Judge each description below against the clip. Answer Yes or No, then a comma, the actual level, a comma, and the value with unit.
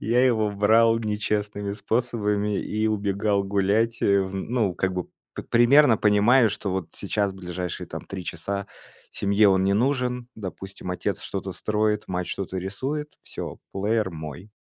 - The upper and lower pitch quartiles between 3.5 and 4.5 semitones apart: No, narrow, 2.5 semitones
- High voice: No, low, 105 Hz